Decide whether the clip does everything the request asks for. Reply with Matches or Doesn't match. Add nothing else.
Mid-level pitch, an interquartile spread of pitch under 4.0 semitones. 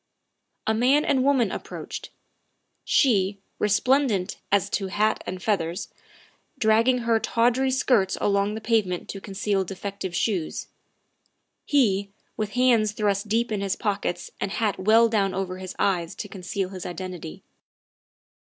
Doesn't match